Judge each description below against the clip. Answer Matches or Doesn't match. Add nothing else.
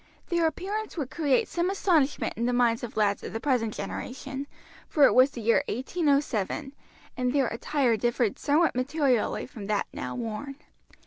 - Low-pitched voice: Doesn't match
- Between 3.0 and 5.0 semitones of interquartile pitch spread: Matches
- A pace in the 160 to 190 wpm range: Matches